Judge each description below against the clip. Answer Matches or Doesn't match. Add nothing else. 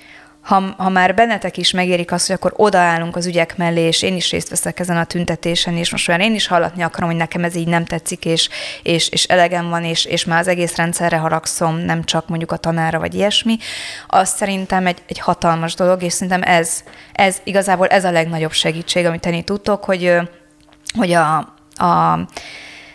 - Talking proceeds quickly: Matches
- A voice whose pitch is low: Doesn't match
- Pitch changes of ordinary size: Doesn't match